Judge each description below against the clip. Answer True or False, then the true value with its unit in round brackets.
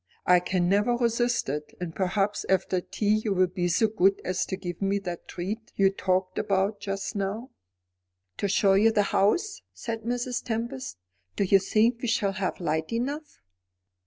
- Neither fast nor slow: True (175 wpm)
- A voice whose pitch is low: False (195 Hz)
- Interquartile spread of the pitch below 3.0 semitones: False (3.5 semitones)